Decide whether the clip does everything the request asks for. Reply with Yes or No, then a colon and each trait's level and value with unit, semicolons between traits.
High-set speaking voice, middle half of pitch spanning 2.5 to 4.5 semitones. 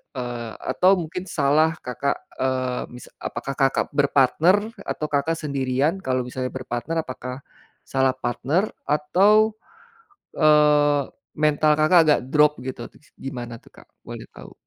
No: medium, 140 Hz; average, 2.9 semitones